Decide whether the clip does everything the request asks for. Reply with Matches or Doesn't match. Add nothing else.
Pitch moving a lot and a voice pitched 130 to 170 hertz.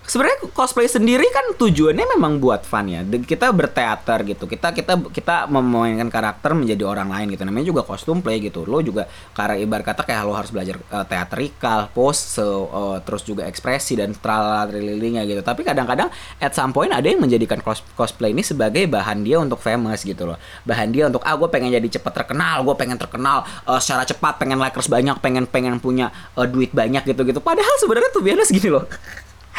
Doesn't match